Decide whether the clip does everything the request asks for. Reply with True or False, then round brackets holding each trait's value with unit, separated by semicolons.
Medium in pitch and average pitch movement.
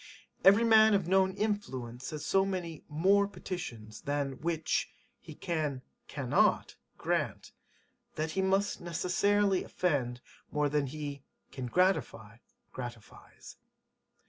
False (160 Hz; 5.9 semitones)